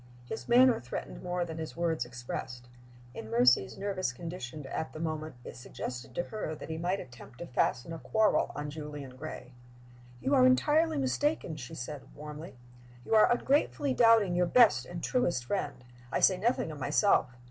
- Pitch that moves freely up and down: Yes, wide, 8.5 semitones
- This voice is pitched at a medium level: Yes, medium, 160 Hz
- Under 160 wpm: No, average, 175 wpm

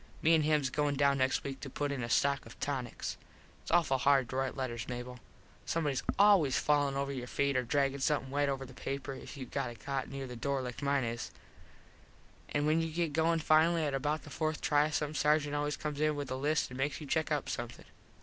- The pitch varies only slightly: Yes, narrow, 2.2 semitones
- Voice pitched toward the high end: No, medium, 140 Hz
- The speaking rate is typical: No, fast, 230 wpm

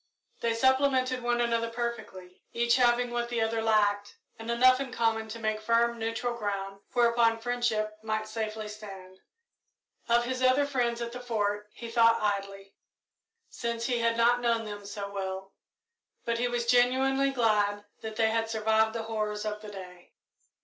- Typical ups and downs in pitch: No, narrow, 2.1 semitones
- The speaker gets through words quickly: No, average, 165 wpm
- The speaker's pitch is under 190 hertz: No, high, 230 Hz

